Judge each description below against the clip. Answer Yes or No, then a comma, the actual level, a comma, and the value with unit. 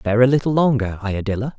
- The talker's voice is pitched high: No, low, 120 Hz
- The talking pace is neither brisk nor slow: Yes, average, 190 wpm